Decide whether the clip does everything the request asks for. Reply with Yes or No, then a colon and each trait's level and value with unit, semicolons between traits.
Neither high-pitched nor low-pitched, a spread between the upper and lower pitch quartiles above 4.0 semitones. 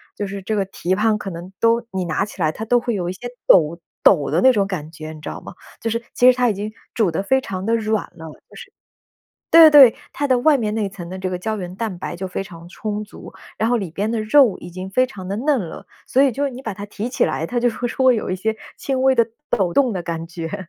No: high, 205 Hz; average, 4.7 semitones